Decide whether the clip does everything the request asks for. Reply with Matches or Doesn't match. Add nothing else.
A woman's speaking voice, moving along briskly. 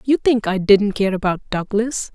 Doesn't match